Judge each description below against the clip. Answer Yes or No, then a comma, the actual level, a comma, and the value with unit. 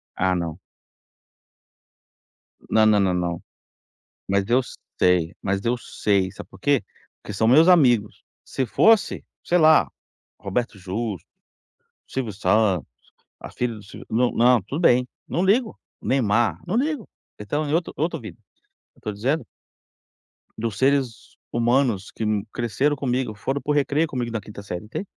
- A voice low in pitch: Yes, low, 115 Hz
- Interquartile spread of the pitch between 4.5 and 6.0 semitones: Yes, wide, 5.5 semitones